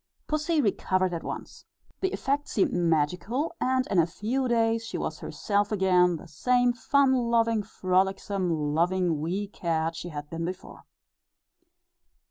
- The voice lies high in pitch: Yes, high, 195 Hz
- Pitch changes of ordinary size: No, wide, 5.8 semitones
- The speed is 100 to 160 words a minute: Yes, average, 140 wpm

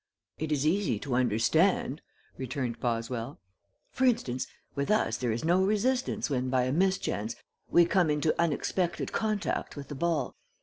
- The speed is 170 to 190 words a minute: No, average, 150 wpm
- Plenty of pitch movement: Yes, wide, 6.6 semitones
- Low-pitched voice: No, medium, 145 Hz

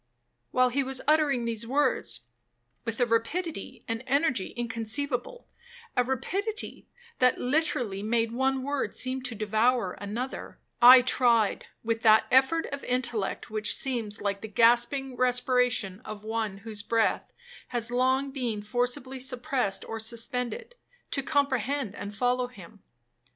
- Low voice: No, high, 245 Hz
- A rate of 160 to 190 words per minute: No, slow, 135 wpm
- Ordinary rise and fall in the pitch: Yes, average, 3.0 semitones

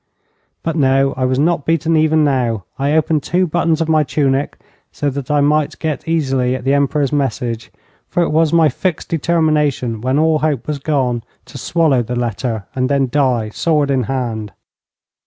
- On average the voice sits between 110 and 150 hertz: Yes, medium, 140 Hz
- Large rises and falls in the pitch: No, average, 3.4 semitones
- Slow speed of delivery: No, average, 180 wpm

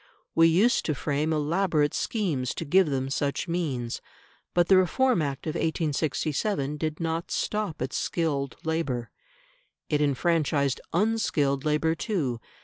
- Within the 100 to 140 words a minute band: Yes, slow, 135 wpm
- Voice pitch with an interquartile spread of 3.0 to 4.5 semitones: Yes, average, 3.4 semitones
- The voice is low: No, medium, 155 Hz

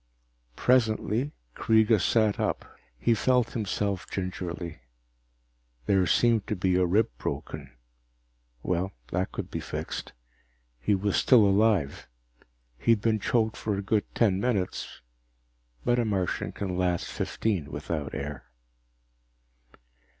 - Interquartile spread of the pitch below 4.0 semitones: Yes, average, 3.5 semitones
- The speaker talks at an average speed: No, slow, 120 wpm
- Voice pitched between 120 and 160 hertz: No, low, 100 Hz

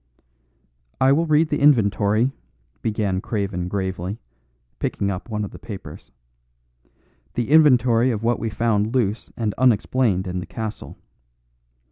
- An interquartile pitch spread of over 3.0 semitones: Yes, average, 3.9 semitones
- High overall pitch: No, low, 110 Hz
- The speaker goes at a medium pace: No, slow, 130 wpm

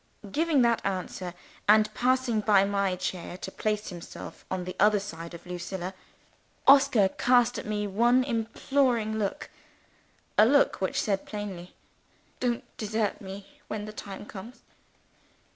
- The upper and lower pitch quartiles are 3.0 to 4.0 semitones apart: Yes, average, 3.6 semitones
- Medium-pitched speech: No, high, 210 Hz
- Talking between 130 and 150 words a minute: Yes, average, 140 wpm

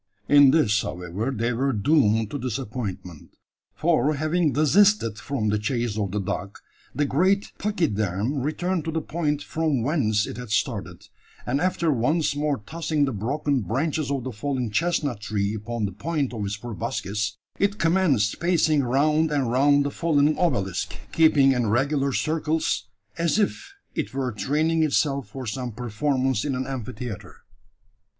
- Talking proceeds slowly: No, average, 155 wpm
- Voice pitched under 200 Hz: Yes, low, 135 Hz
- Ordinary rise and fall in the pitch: No, wide, 5.8 semitones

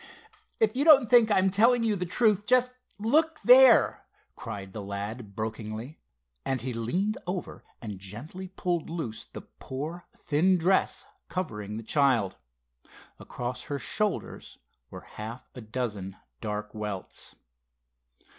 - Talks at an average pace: No, slow, 130 wpm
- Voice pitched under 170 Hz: Yes, medium, 140 Hz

